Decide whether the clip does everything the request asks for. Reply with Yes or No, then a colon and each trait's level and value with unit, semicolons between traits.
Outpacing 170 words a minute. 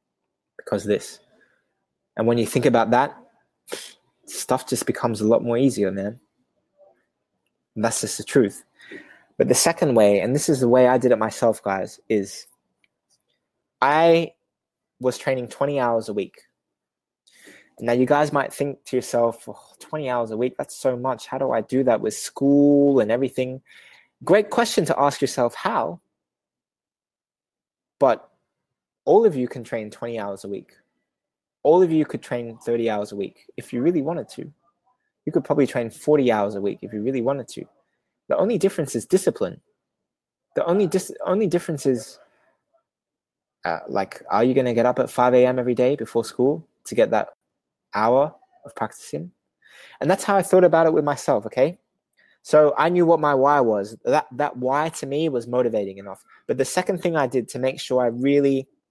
Yes: average, 180 wpm